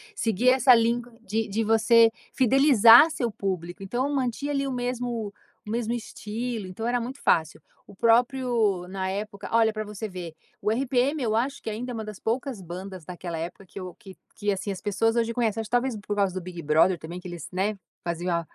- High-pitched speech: Yes, high, 220 Hz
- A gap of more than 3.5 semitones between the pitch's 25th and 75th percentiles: Yes, average, 4.3 semitones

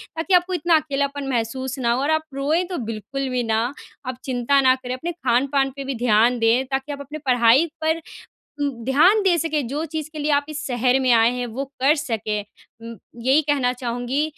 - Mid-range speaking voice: No, very high, 270 Hz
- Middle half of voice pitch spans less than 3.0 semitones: No, average, 3.6 semitones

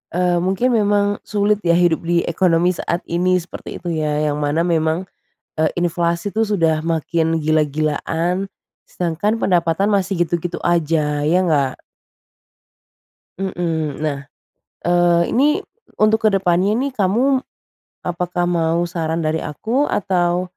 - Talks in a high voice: No, medium, 175 Hz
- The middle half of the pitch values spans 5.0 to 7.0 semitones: No, average, 2.9 semitones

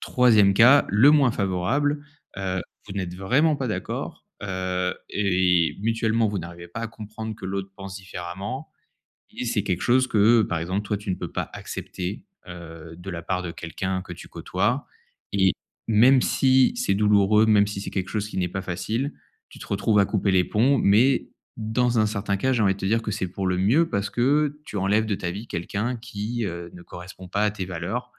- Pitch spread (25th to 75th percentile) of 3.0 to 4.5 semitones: Yes, average, 3.5 semitones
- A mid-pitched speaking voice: No, low, 100 Hz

